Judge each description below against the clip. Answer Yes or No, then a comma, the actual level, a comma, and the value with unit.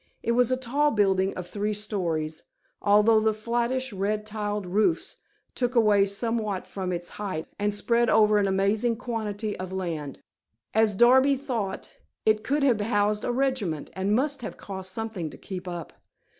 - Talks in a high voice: Yes, high, 210 Hz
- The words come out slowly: No, average, 165 wpm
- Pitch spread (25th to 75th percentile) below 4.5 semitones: Yes, average, 3.5 semitones